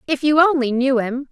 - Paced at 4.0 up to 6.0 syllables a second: Yes, 5.2 syllables/s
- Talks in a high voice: Yes, very high, 270 Hz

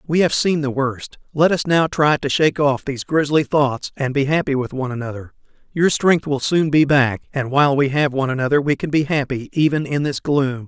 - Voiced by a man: Yes, male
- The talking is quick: Yes, fast, 230 wpm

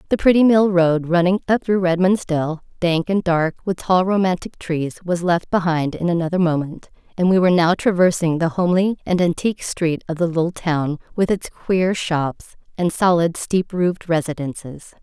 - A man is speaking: No, female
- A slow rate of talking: No, average, 180 wpm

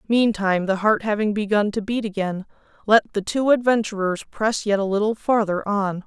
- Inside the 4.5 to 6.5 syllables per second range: Yes, 5.3 syllables/s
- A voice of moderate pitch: No, high, 210 Hz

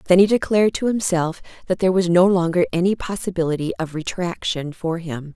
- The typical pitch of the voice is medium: Yes, medium, 175 Hz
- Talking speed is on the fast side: No, average, 180 wpm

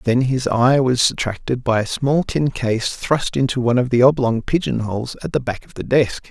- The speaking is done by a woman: No, male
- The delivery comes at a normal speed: No, fast, 230 wpm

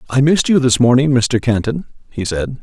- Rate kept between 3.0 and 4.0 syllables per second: No, 5.5 syllables/s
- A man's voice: Yes, male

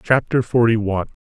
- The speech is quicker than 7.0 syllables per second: No, 6.1 syllables/s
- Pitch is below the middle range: Yes, low, 115 Hz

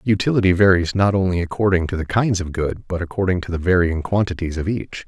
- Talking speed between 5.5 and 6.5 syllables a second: Yes, 6.0 syllables/s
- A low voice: Yes, very low, 90 Hz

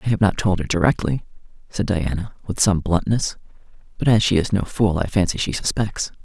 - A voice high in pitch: No, very low, 95 Hz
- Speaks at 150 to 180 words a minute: No, average, 200 wpm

